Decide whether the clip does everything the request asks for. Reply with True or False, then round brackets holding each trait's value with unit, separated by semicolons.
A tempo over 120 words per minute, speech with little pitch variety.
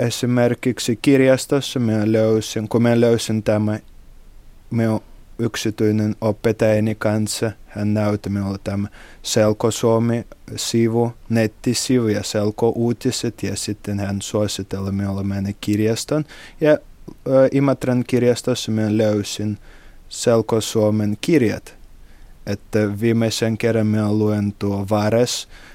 False (105 wpm; 2.1 semitones)